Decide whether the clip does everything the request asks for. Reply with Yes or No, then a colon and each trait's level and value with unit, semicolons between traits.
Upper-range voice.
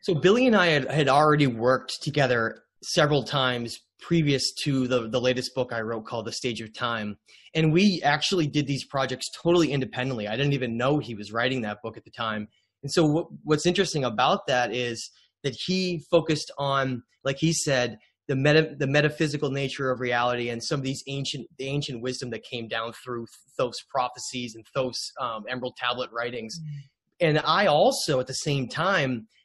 No: low, 135 Hz